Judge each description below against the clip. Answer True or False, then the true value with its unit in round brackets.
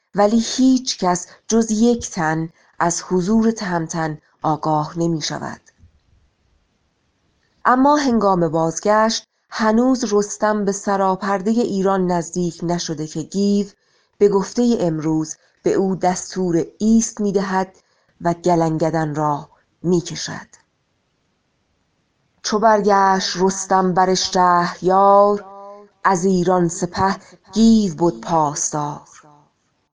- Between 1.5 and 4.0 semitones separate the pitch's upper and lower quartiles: True (3.6 semitones)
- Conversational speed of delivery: False (100 wpm)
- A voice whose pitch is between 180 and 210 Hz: True (190 Hz)